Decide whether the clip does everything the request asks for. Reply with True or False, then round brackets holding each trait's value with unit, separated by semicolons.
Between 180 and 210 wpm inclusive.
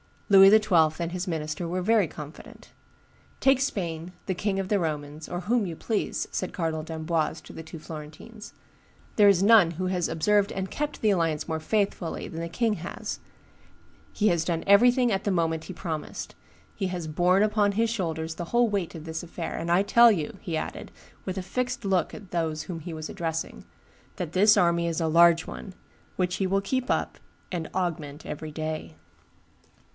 True (190 wpm)